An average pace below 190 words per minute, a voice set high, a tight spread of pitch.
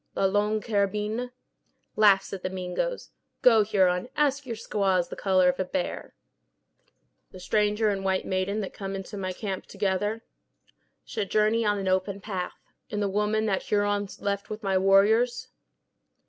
Yes: average, 160 wpm; high, 200 Hz; narrow, 2.0 semitones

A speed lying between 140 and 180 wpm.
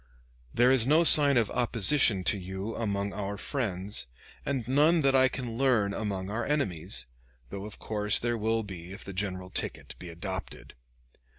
Yes: average, 170 wpm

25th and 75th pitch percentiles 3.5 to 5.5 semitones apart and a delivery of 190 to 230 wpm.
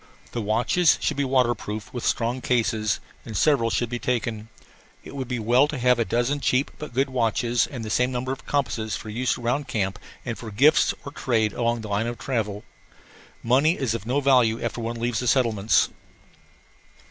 No: narrow, 2.6 semitones; average, 195 wpm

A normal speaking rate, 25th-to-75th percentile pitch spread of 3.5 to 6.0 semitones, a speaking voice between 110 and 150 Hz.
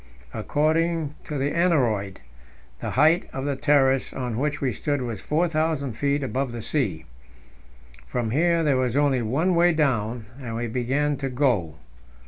Yes: average, 155 wpm; average, 3.8 semitones; low, 135 Hz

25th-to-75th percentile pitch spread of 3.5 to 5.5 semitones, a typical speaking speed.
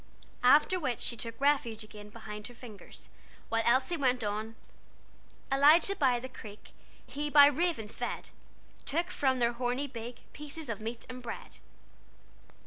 Yes: average, 4.1 semitones; average, 145 wpm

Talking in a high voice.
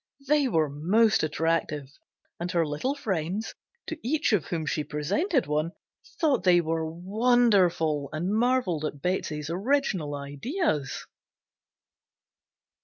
No: medium, 175 Hz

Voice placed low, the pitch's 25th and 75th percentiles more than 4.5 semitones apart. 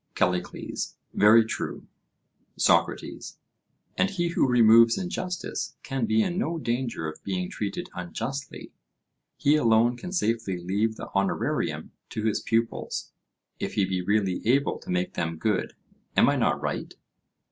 Yes: low, 110 Hz; wide, 5.4 semitones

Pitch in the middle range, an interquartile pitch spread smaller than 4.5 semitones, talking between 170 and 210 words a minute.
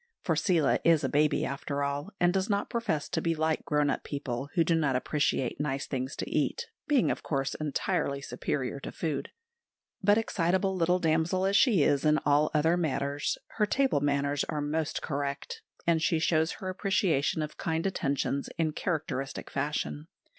Yes: medium, 155 Hz; average, 3.7 semitones; average, 175 wpm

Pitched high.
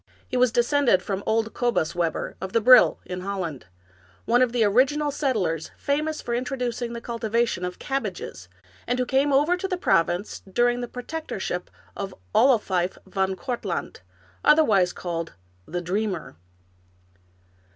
Yes: high, 230 Hz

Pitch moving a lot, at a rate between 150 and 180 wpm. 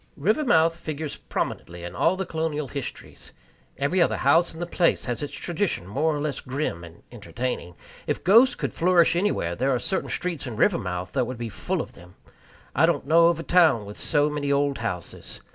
No: wide, 6.2 semitones; average, 195 wpm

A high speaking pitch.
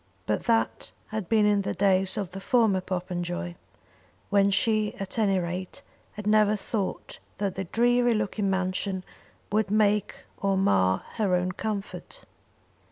Yes: high, 200 Hz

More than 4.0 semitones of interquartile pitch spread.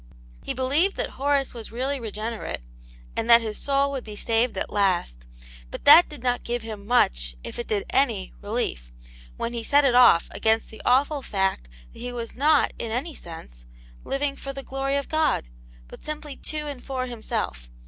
Yes: average, 4.5 semitones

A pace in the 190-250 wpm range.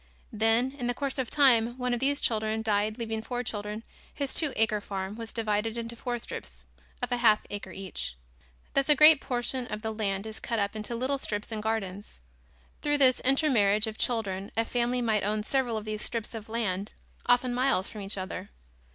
Yes: average, 200 wpm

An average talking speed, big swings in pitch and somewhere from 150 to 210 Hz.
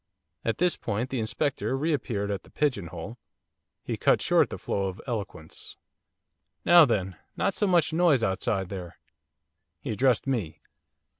No: average, 155 wpm; wide, 6.8 semitones; low, 115 Hz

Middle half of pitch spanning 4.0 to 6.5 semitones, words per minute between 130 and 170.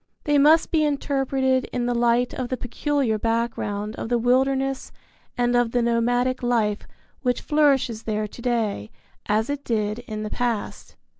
No: average, 2.8 semitones; average, 160 wpm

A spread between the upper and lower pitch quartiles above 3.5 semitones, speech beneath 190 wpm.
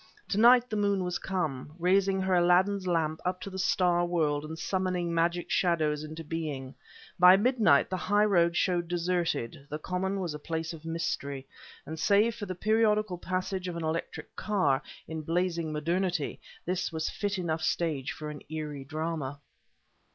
No: average, 3.1 semitones; average, 170 wpm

